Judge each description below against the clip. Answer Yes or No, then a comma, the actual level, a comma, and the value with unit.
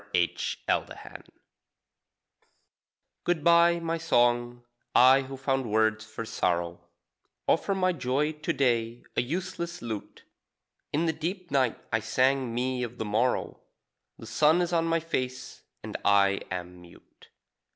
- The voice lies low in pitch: Yes, low, 130 Hz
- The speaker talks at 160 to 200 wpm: No, average, 140 wpm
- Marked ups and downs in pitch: Yes, wide, 6.5 semitones